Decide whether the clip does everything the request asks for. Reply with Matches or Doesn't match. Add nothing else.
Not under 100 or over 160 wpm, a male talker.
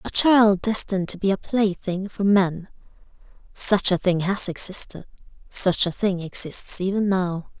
Doesn't match